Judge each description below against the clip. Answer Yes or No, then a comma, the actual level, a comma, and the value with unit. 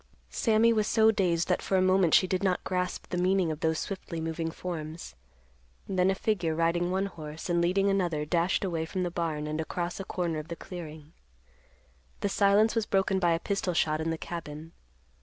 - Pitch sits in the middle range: Yes, medium, 175 Hz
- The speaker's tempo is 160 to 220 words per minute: Yes, average, 200 wpm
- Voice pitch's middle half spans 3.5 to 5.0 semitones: No, average, 2.9 semitones